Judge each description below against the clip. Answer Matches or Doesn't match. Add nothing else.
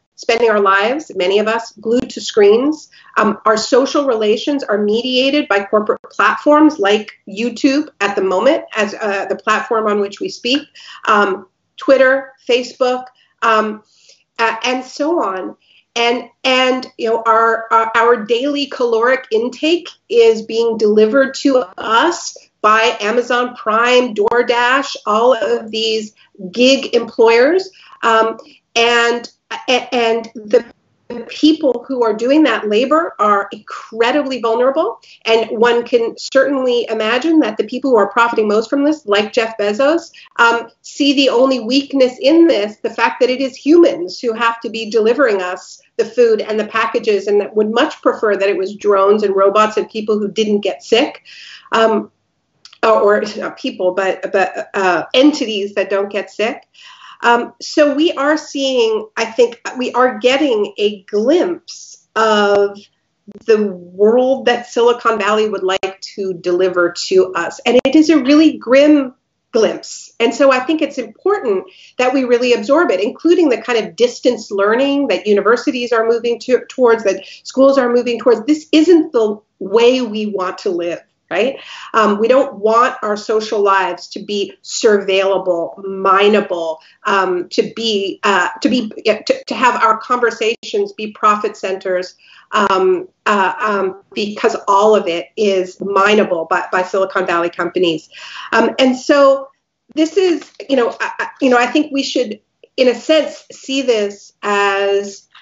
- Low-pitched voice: Doesn't match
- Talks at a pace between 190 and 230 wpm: Doesn't match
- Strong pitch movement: Doesn't match